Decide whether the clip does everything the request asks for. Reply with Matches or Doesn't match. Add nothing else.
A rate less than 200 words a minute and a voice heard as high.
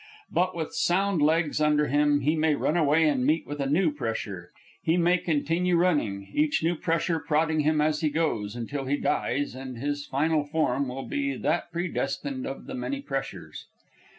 Doesn't match